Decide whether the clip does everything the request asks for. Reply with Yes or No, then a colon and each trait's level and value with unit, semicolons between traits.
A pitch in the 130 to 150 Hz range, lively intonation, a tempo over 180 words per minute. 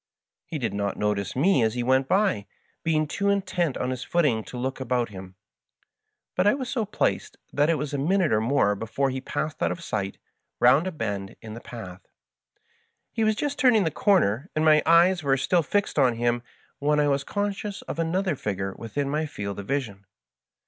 Yes: medium, 140 Hz; wide, 7.5 semitones; average, 200 wpm